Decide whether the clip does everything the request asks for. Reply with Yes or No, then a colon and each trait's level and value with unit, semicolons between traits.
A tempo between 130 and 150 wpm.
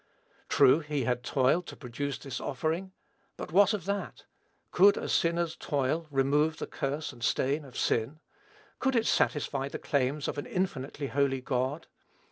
No: average, 160 wpm